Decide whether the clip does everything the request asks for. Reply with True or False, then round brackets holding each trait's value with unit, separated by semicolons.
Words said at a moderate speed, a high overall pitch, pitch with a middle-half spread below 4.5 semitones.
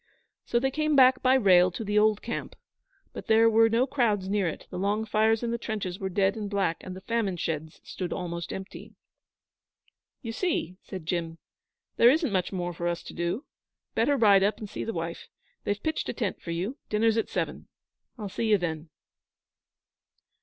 True (195 wpm; 205 Hz; 4.1 semitones)